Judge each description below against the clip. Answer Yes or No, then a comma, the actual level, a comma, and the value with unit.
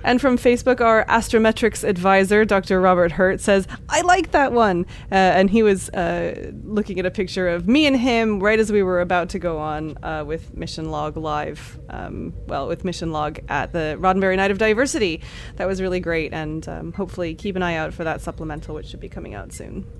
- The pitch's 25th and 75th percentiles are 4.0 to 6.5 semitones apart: Yes, average, 4.6 semitones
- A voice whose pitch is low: No, medium, 185 Hz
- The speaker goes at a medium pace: No, fast, 215 wpm